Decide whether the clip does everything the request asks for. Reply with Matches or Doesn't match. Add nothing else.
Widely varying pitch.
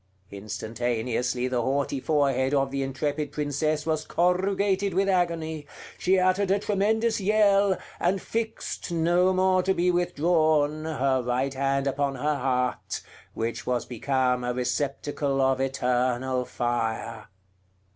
Matches